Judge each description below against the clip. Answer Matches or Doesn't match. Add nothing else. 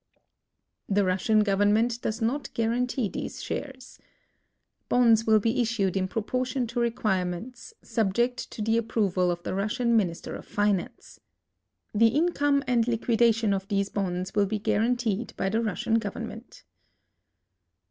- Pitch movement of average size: Matches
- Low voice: Doesn't match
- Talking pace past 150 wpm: Doesn't match